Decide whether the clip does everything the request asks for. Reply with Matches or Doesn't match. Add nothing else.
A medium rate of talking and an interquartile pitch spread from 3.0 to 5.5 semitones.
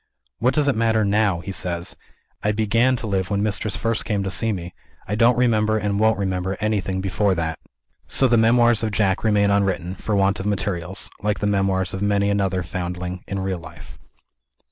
Doesn't match